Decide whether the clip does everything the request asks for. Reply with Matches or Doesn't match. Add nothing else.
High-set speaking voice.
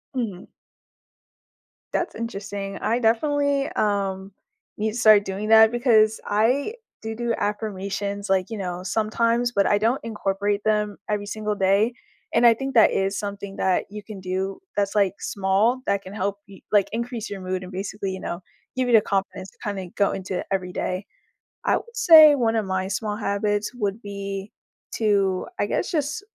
Matches